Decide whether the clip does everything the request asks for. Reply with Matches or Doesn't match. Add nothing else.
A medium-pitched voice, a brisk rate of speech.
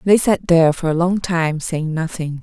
Matches